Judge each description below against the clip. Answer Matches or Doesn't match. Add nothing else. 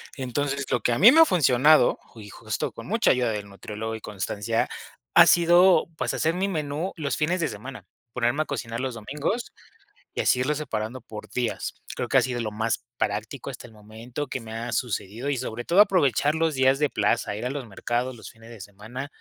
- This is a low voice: Matches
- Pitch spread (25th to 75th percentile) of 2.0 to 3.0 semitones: Doesn't match